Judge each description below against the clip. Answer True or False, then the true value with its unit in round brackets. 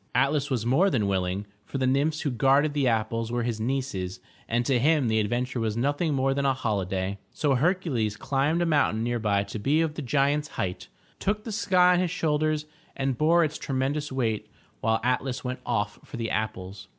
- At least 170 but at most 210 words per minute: True (200 wpm)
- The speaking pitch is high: False (130 Hz)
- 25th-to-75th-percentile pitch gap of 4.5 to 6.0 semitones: True (5.0 semitones)